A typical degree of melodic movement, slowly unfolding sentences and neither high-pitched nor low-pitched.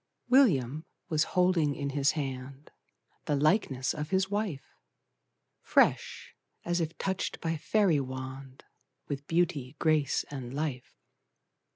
Yes: average, 4.3 semitones; slow, 115 wpm; medium, 150 Hz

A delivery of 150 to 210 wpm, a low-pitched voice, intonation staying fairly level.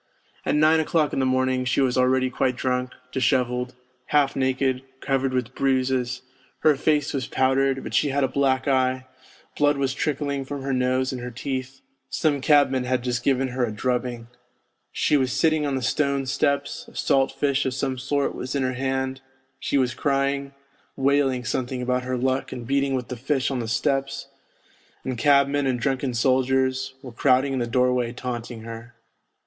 Yes: average, 180 wpm; low, 130 Hz; narrow, 1.6 semitones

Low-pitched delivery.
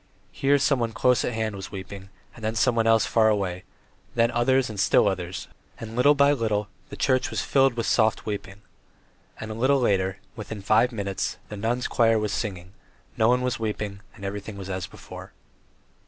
Yes: low, 110 Hz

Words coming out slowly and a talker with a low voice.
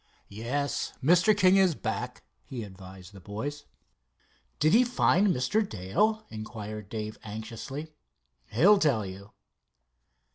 Yes: slow, 115 wpm; low, 130 Hz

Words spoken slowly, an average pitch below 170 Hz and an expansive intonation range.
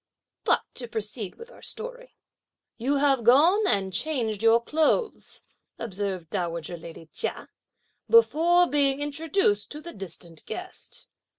No: slow, 125 wpm; very high, 250 Hz; wide, 8.3 semitones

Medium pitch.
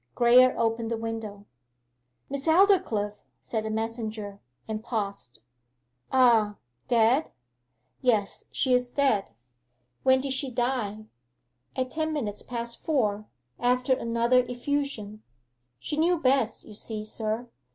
No: high, 235 Hz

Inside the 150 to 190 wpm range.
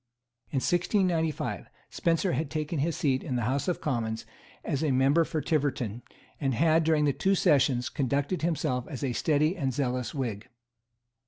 Yes: average, 155 wpm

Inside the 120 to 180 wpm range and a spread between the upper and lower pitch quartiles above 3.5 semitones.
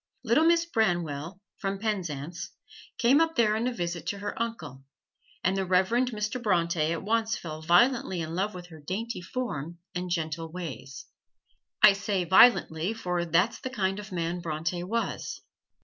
Yes: average, 165 wpm; average, 4.9 semitones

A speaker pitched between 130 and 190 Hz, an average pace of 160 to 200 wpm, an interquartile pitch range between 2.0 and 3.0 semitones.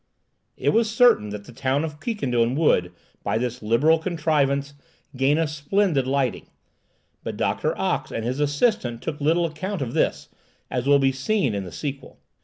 No: medium, 140 Hz; average, 170 wpm; average, 4.5 semitones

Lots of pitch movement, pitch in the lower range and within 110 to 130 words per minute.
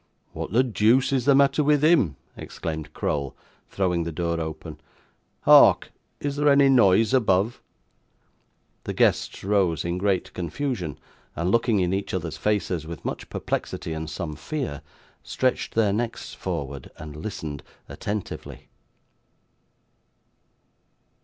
Yes: wide, 7.1 semitones; very low, 95 Hz; slow, 125 wpm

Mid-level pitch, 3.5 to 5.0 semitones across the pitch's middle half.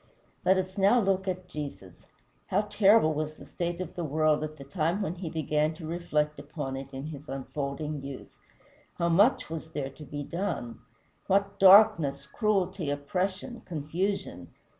Yes: medium, 160 Hz; average, 4.5 semitones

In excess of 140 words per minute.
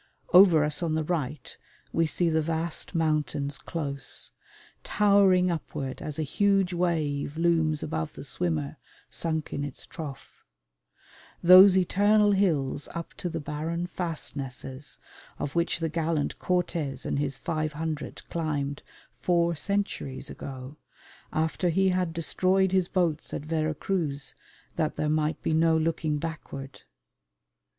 No: slow, 135 wpm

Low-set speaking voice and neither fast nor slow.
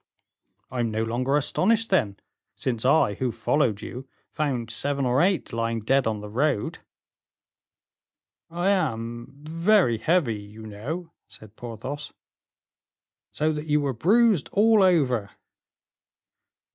No: low, 130 Hz; slow, 125 wpm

